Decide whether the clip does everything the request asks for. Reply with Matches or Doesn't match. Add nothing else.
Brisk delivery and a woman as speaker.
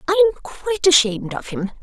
Doesn't match